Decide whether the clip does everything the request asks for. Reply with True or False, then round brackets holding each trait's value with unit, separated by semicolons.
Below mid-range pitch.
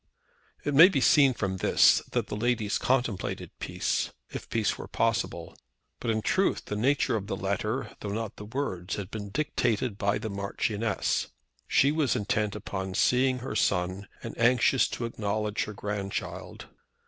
True (110 Hz)